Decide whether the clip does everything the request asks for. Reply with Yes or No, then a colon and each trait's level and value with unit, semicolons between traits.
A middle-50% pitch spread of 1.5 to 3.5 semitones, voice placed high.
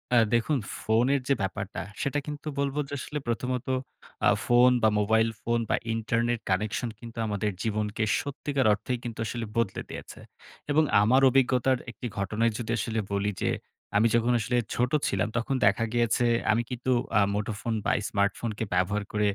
No: average, 2.9 semitones; low, 115 Hz